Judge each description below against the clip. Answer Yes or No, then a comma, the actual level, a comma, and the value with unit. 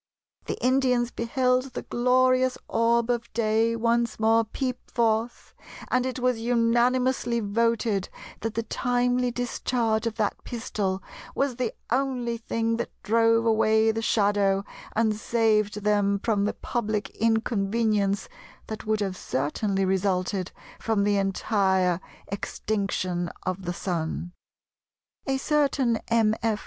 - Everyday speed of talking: No, slow, 125 wpm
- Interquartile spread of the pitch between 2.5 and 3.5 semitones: Yes, average, 2.8 semitones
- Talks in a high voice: Yes, high, 225 Hz